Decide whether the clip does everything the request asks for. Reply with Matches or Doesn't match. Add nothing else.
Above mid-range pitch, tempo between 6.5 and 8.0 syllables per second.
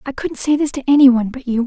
Matches